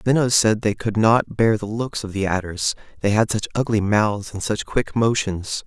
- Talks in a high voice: No, low, 105 Hz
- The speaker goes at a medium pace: No, fast, 210 wpm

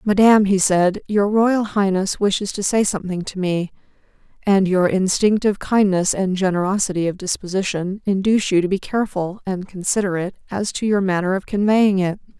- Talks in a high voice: Yes, high, 195 Hz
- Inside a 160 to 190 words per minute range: Yes, average, 165 wpm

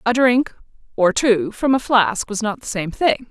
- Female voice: Yes, female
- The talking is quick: Yes, fast, 220 wpm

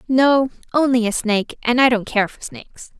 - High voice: Yes, high, 245 Hz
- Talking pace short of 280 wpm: Yes, average, 200 wpm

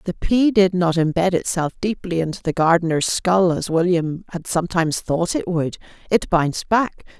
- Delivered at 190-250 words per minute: No, average, 175 wpm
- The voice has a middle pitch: Yes, medium, 175 Hz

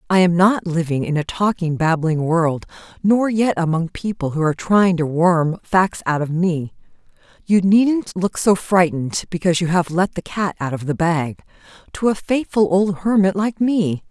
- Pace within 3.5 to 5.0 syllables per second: Yes, 4.6 syllables/s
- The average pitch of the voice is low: No, medium, 180 Hz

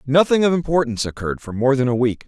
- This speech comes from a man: Yes, male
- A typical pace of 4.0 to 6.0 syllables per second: No, 7.0 syllables/s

